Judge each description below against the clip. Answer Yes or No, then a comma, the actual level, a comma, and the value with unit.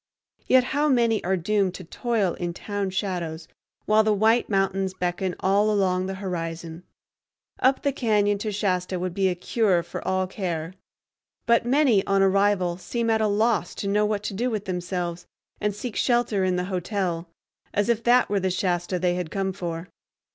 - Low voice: No, high, 195 Hz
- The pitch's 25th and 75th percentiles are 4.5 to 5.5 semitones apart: No, average, 3.0 semitones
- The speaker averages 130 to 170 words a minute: No, average, 185 wpm